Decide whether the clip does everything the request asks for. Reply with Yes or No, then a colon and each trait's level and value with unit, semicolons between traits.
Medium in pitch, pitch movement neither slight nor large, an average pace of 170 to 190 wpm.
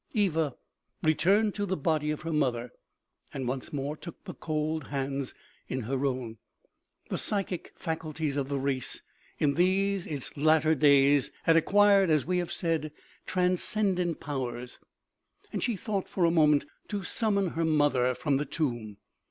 No: medium, 155 Hz; average, 4.6 semitones; average, 160 wpm